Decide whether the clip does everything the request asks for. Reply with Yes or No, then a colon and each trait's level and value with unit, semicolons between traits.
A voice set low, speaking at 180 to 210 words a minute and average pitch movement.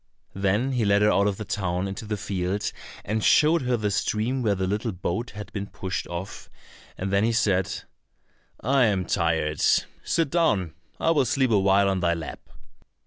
Yes: low, 100 Hz; average, 185 wpm; average, 3.5 semitones